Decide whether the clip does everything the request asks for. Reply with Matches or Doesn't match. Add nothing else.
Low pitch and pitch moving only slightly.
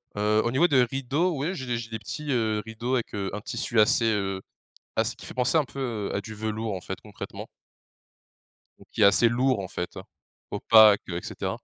Doesn't match